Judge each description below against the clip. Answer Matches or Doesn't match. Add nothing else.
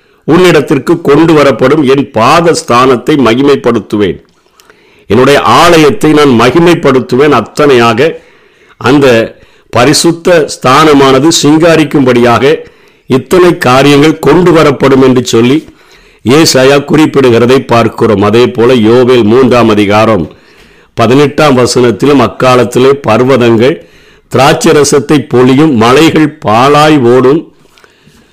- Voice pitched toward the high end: Doesn't match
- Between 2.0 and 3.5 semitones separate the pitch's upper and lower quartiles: Doesn't match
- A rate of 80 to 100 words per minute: Matches